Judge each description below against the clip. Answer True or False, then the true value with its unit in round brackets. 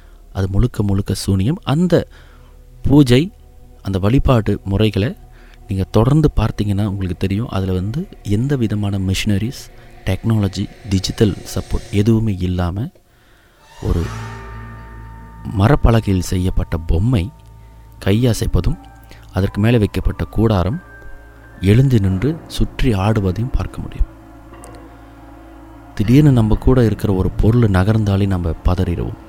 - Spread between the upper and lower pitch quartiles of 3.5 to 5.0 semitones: True (3.9 semitones)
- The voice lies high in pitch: False (105 Hz)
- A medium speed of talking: True (100 wpm)